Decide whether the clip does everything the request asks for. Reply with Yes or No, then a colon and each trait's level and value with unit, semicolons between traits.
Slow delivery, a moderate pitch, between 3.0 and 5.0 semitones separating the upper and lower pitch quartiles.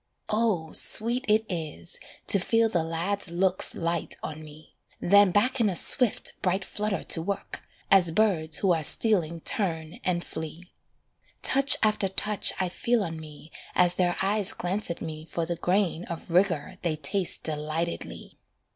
No: average, 160 wpm; medium, 180 Hz; average, 3.9 semitones